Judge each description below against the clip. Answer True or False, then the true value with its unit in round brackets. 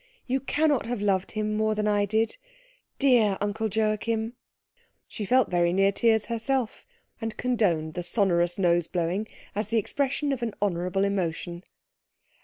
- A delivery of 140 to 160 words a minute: True (150 wpm)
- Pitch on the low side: False (210 Hz)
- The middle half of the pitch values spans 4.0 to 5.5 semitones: False (3.5 semitones)